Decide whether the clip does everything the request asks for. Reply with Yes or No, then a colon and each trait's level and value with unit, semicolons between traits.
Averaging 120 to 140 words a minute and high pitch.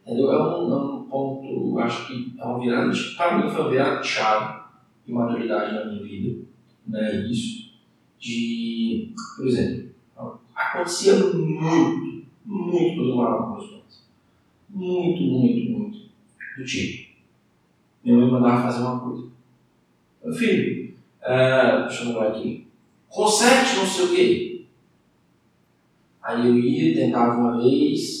No: average, 135 wpm; low, 125 Hz